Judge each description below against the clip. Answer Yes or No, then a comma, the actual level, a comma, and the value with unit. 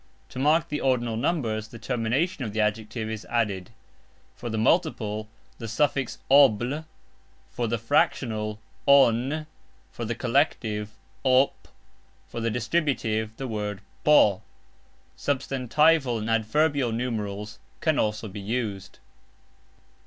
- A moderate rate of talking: No, slow, 120 wpm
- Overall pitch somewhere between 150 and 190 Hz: No, low, 115 Hz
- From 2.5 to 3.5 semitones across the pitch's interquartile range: No, average, 4.0 semitones